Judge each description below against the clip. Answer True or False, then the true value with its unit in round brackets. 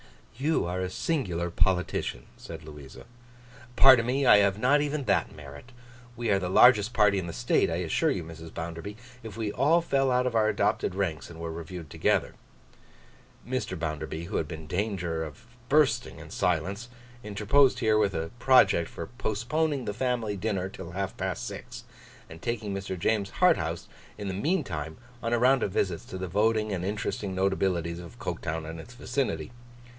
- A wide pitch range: True (5.9 semitones)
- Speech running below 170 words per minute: False (180 wpm)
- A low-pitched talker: True (100 Hz)